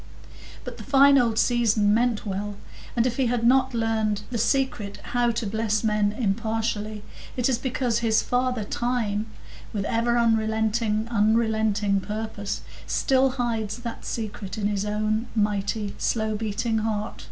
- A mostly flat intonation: Yes, narrow, 2.1 semitones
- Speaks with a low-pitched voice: No, high, 220 Hz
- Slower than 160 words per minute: Yes, average, 140 wpm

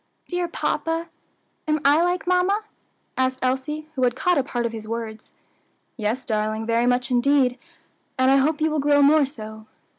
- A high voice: Yes, very high, 265 Hz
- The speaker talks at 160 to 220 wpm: Yes, average, 175 wpm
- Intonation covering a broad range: No, average, 4.6 semitones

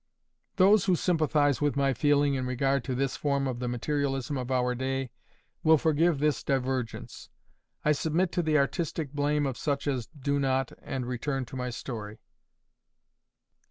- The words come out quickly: No, average, 160 wpm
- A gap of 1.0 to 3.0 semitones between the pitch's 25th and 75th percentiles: Yes, narrow, 2.5 semitones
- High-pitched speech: No, medium, 140 Hz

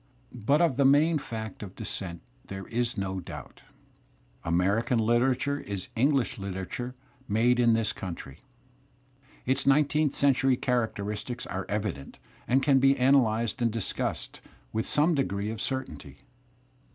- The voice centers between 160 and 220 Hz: No, low, 120 Hz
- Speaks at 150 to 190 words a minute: No, slow, 135 wpm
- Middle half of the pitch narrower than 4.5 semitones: No, average, 4.8 semitones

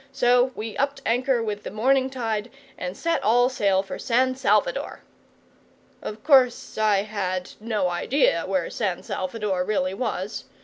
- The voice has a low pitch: No, high, 220 Hz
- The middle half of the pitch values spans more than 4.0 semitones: Yes, average, 4.8 semitones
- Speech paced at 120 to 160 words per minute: Yes, average, 145 wpm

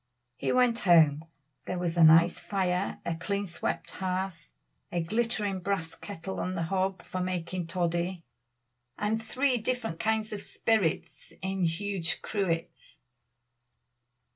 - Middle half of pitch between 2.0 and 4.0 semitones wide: Yes, average, 3.2 semitones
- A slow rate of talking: Yes, slow, 130 wpm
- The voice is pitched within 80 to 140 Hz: No, medium, 185 Hz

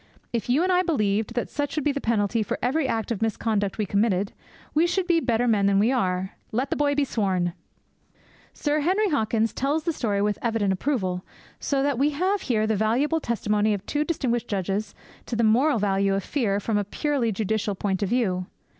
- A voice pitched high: Yes, high, 225 Hz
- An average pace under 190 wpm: No, fast, 205 wpm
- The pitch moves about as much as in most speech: No, wide, 5.8 semitones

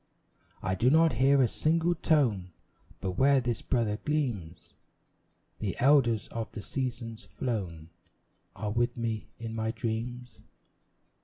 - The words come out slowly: Yes, slow, 130 wpm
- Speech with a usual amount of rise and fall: Yes, average, 3.9 semitones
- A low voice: Yes, low, 115 Hz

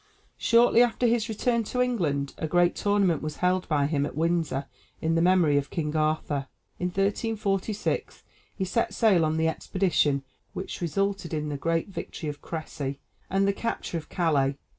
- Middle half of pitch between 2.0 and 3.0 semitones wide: No, average, 4.6 semitones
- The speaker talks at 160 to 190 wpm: Yes, average, 165 wpm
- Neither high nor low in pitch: Yes, medium, 170 Hz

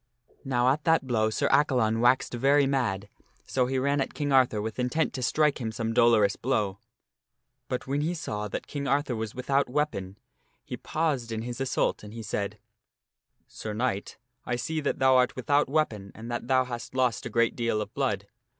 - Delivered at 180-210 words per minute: Yes, average, 195 wpm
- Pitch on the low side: Yes, low, 125 Hz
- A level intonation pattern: No, average, 3.6 semitones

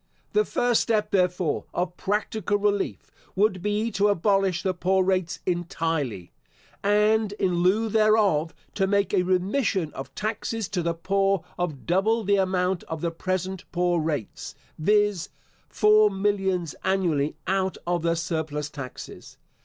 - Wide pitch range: No, average, 3.3 semitones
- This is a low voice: No, high, 190 Hz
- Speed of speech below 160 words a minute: Yes, average, 140 wpm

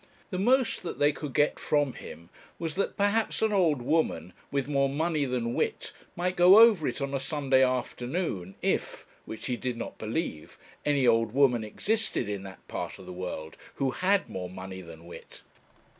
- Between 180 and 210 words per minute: Yes, average, 185 wpm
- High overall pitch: No, low, 135 Hz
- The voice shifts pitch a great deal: Yes, wide, 7.5 semitones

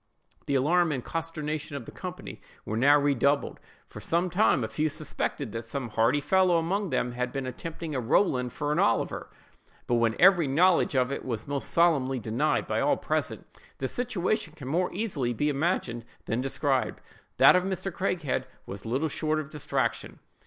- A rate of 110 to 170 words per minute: No, average, 180 wpm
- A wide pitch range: No, average, 4.9 semitones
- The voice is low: No, medium, 145 Hz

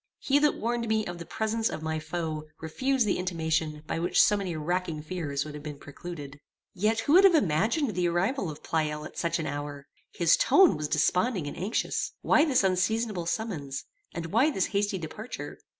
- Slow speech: No, average, 195 wpm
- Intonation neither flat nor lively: No, wide, 6.1 semitones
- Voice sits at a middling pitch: Yes, medium, 175 Hz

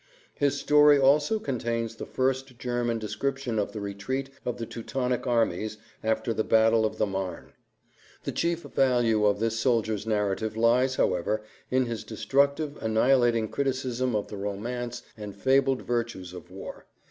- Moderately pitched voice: No, low, 115 Hz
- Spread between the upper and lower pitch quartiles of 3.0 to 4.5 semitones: Yes, average, 3.4 semitones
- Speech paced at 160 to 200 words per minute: No, average, 150 wpm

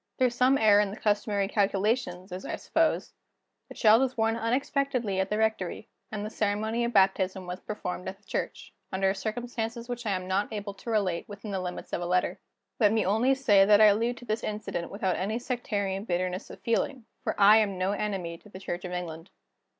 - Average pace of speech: No, fast, 210 wpm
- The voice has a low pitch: No, high, 205 Hz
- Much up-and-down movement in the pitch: No, average, 3.0 semitones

